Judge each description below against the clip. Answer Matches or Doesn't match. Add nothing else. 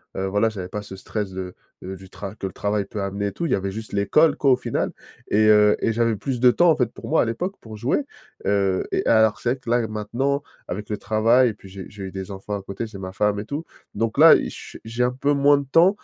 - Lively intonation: Doesn't match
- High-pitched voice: Doesn't match